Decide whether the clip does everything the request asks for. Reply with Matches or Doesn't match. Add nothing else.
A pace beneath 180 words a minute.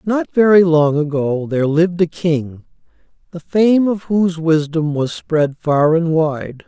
Matches